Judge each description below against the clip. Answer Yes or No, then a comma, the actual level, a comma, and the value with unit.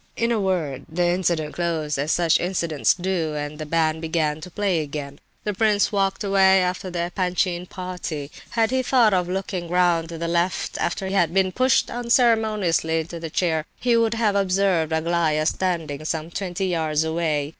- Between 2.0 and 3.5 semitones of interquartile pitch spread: Yes, average, 3.2 semitones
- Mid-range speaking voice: Yes, medium, 175 Hz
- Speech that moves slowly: No, average, 185 wpm